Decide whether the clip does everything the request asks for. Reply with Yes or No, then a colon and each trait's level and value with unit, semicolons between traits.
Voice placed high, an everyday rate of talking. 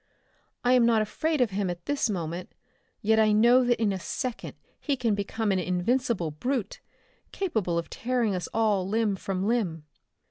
Yes: high, 215 Hz; average, 175 wpm